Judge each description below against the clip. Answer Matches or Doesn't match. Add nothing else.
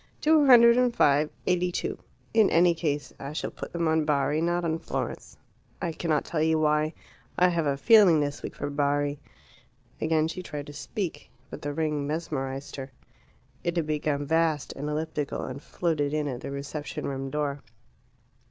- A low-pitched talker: Doesn't match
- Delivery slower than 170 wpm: Doesn't match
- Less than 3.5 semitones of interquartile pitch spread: Matches